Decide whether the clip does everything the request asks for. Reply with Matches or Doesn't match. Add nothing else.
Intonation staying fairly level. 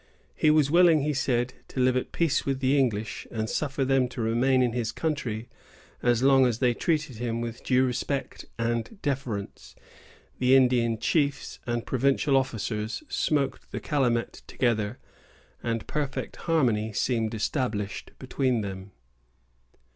Doesn't match